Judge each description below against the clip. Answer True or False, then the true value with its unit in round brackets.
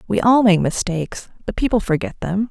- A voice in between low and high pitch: False (205 Hz)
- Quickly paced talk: False (190 wpm)